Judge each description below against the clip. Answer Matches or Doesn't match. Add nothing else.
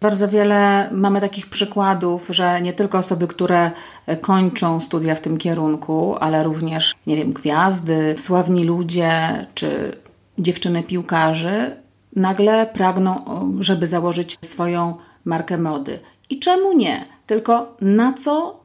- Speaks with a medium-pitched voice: Matches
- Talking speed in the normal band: Matches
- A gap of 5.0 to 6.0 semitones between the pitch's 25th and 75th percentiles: Doesn't match